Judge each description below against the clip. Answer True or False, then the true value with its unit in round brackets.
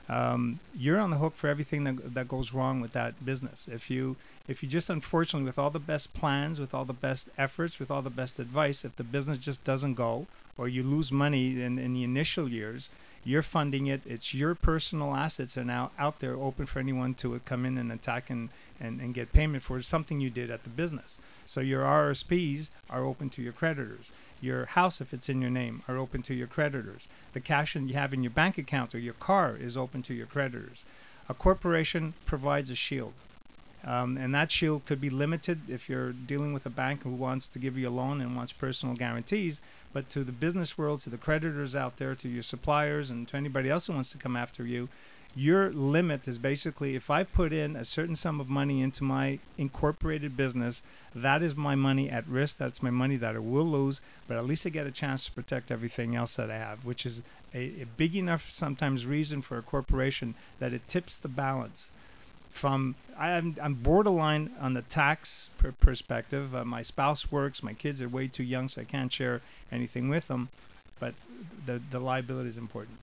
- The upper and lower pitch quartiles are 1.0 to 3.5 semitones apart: True (2.9 semitones)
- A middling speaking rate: False (215 wpm)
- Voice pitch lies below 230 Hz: True (135 Hz)